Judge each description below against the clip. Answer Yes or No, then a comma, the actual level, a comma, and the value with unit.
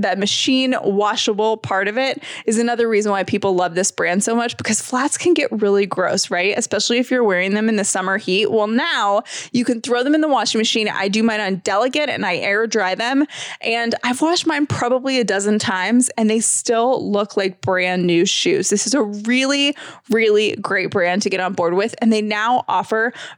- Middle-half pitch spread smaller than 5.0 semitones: Yes, average, 3.8 semitones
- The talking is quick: Yes, fast, 215 wpm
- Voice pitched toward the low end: No, high, 220 Hz